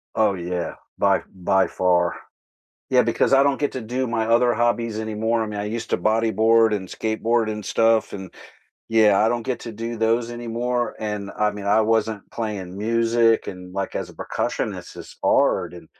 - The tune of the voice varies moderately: No, narrow, 2.2 semitones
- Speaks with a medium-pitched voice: No, low, 110 Hz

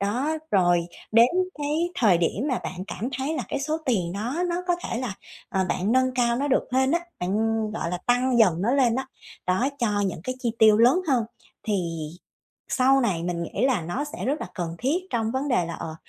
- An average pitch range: No, wide, 5.8 semitones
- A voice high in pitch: Yes, high, 235 Hz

